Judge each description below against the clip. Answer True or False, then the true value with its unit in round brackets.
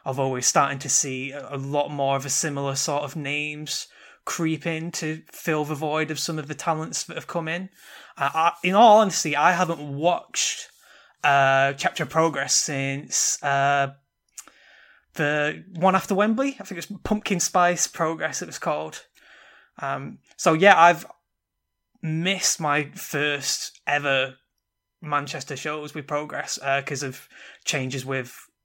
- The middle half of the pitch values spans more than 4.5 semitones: False (3.3 semitones)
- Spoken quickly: False (155 wpm)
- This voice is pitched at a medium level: True (150 Hz)